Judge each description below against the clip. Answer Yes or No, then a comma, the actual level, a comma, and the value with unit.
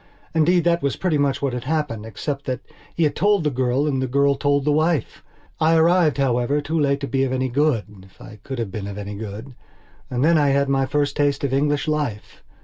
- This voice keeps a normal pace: No, fast, 235 wpm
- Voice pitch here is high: No, medium, 140 Hz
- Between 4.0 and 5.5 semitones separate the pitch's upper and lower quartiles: No, average, 3.2 semitones